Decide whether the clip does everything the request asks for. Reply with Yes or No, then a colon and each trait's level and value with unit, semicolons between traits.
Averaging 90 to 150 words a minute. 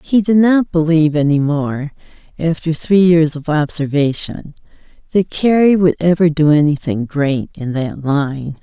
Yes: average, 145 wpm